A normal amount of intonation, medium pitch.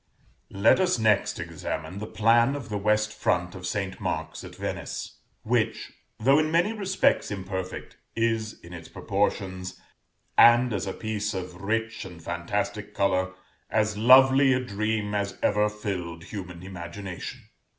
No: average, 3.6 semitones; low, 105 Hz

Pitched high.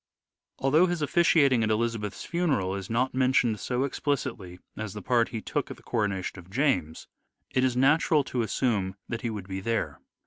No: low, 115 Hz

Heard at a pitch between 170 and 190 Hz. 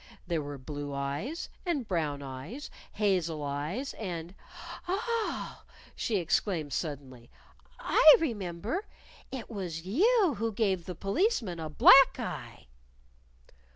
Yes: medium, 185 Hz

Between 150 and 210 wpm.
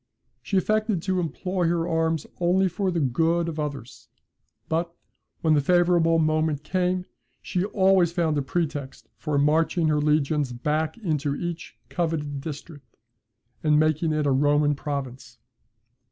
No: average, 140 wpm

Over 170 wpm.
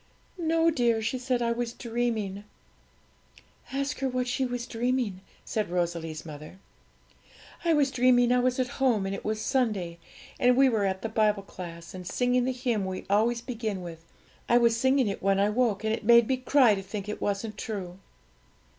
Yes: average, 190 wpm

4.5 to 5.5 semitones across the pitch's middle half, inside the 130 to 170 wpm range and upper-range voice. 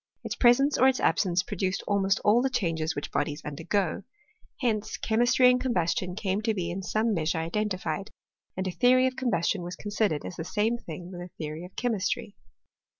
No: average, 5.2 semitones; average, 185 wpm; high, 195 Hz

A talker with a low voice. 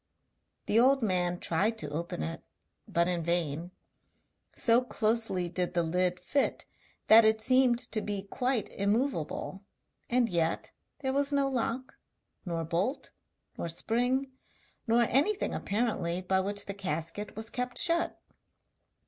No: high, 210 Hz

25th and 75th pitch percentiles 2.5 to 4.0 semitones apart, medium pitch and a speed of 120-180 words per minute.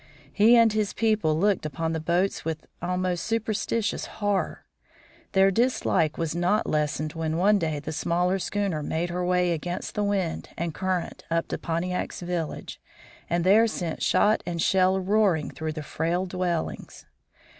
Yes: average, 3.5 semitones; medium, 180 Hz; average, 155 wpm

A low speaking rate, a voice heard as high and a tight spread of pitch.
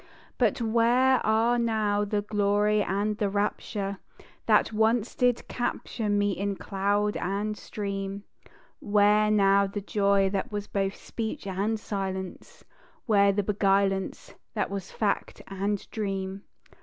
Yes: slow, 130 wpm; high, 205 Hz; narrow, 1.4 semitones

